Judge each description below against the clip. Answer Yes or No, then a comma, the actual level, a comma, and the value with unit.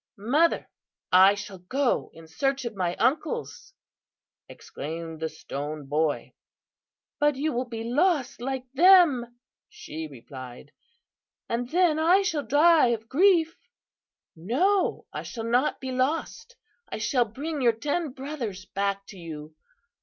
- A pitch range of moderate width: No, wide, 8.3 semitones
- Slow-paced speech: Yes, slow, 130 wpm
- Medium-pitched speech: No, high, 245 Hz